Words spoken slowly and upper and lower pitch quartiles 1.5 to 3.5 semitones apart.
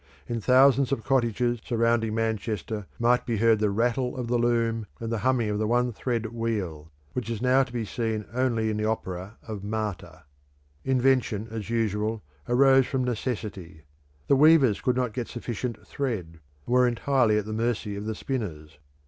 No: average, 175 wpm; narrow, 2.6 semitones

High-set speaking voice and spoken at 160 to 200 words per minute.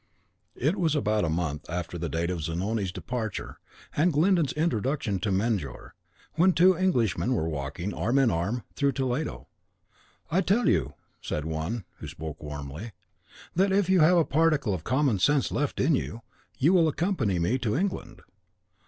No: low, 115 Hz; average, 170 wpm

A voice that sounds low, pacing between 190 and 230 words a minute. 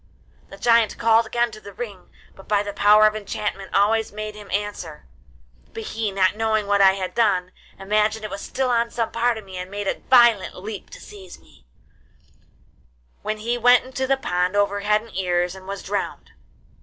No: high, 210 Hz; average, 195 wpm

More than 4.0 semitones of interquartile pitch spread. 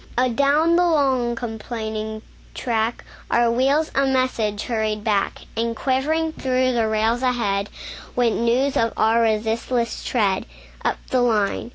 No: average, 2.9 semitones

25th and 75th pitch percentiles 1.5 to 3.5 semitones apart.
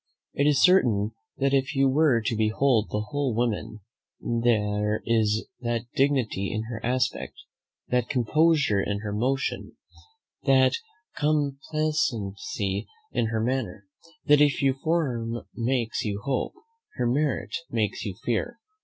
No: average, 4.1 semitones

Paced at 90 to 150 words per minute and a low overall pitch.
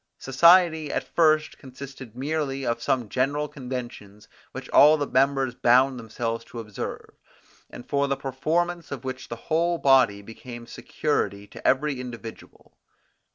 Yes: average, 140 wpm; low, 130 Hz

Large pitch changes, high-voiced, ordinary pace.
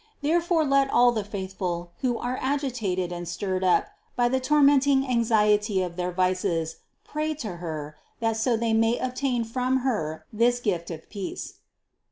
Yes: wide, 6.0 semitones; high, 225 Hz; average, 165 wpm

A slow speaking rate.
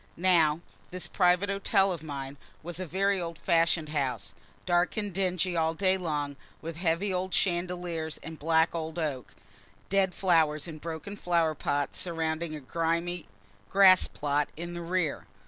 No: average, 160 wpm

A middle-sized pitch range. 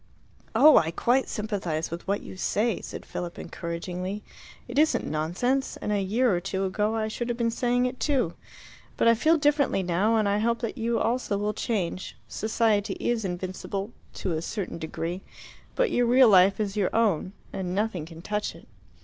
Yes: average, 4.2 semitones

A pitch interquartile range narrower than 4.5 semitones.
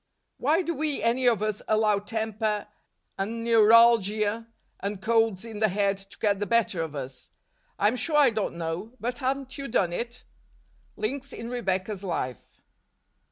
Yes: average, 3.1 semitones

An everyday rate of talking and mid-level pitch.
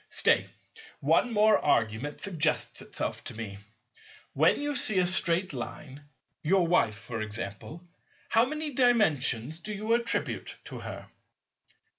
No: slow, 125 wpm; medium, 170 Hz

